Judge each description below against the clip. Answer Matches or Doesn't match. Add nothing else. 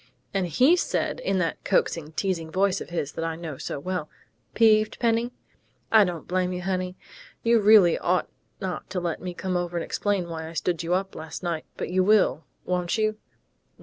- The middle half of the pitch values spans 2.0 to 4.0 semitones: Matches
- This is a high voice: Doesn't match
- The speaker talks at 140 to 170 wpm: Doesn't match